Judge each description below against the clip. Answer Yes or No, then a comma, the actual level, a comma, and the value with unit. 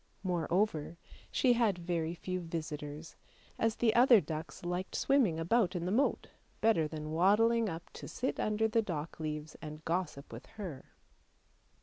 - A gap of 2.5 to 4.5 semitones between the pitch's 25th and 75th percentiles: No, wide, 5.6 semitones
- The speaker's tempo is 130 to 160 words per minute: Yes, average, 150 wpm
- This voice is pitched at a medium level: Yes, medium, 175 Hz